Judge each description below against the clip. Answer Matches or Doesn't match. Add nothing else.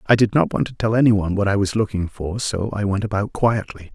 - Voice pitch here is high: Doesn't match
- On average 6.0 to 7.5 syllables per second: Matches